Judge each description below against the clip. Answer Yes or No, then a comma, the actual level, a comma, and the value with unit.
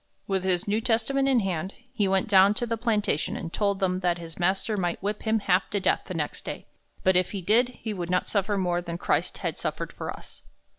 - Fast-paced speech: Yes, fast, 235 wpm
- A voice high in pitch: Yes, high, 195 Hz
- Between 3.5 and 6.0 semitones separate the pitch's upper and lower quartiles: No, average, 3.1 semitones